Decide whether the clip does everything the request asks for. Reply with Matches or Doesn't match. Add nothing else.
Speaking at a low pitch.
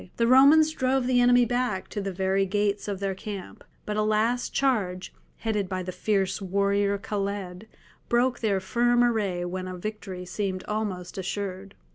Doesn't match